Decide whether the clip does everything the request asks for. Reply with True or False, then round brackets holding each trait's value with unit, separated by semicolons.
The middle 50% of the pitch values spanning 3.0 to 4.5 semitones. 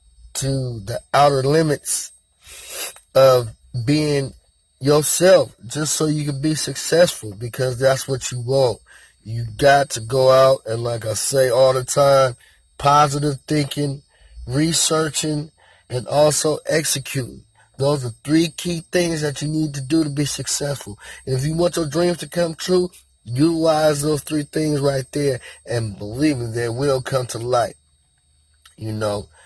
True (3.9 semitones)